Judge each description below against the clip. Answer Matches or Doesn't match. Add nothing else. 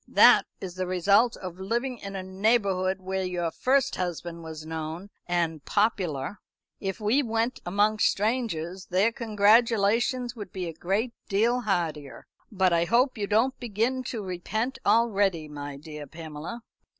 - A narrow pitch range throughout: Doesn't match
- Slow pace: Doesn't match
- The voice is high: Matches